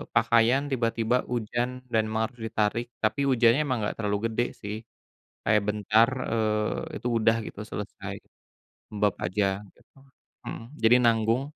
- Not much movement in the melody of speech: Yes, narrow, 1.9 semitones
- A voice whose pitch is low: Yes, low, 110 Hz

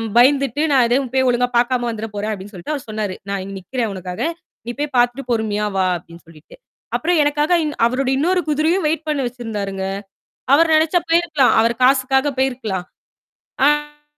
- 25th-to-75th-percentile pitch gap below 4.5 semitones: No, wide, 5.6 semitones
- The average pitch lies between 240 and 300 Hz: Yes, very high, 255 Hz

